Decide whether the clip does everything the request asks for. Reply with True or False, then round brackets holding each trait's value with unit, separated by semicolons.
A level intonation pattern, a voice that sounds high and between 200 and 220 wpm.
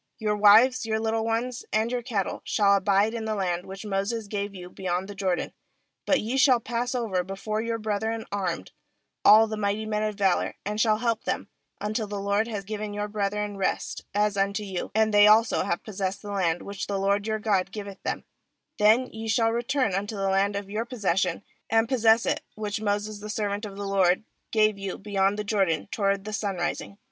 True (1.9 semitones; 210 Hz; 205 wpm)